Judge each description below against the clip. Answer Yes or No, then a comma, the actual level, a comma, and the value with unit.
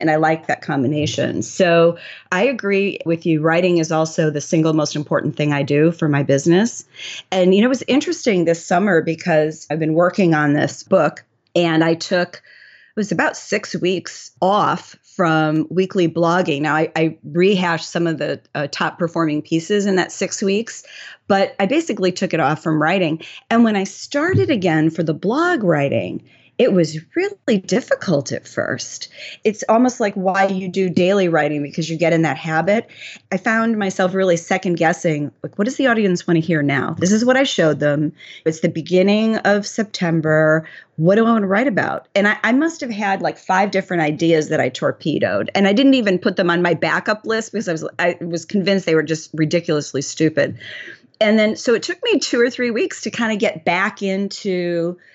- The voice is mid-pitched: Yes, medium, 180 Hz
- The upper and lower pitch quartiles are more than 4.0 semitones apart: Yes, average, 4.4 semitones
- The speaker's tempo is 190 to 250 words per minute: Yes, average, 200 wpm